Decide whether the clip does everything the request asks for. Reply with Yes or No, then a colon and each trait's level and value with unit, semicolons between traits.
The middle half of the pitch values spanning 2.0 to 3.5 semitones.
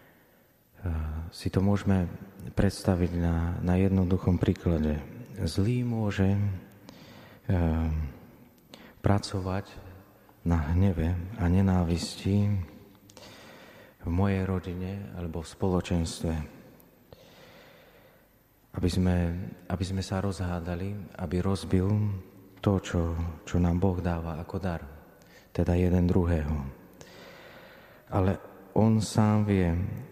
Yes: narrow, 2.4 semitones